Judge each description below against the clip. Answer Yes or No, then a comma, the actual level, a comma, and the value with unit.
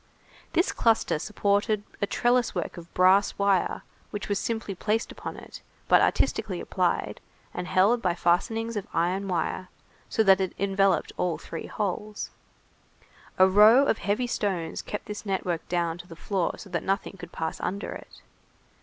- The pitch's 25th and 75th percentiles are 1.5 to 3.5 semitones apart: Yes, average, 2.9 semitones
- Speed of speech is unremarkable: Yes, average, 165 wpm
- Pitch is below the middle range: No, high, 195 Hz